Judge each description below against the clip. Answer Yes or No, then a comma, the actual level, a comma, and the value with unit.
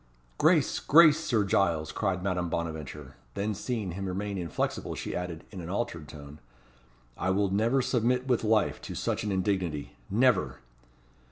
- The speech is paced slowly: No, average, 155 wpm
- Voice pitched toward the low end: Yes, very low, 95 Hz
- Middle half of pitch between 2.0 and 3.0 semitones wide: No, average, 4.3 semitones